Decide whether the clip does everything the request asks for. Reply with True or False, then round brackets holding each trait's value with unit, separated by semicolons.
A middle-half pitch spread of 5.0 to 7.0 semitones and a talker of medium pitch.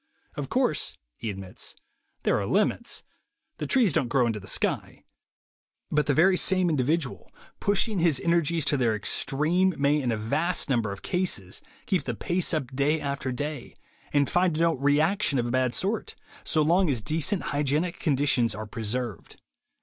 True (5.5 semitones; 145 Hz)